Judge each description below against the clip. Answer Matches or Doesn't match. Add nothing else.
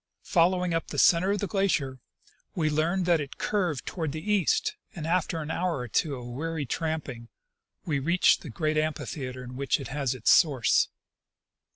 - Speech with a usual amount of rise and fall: Matches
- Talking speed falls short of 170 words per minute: Doesn't match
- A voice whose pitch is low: Doesn't match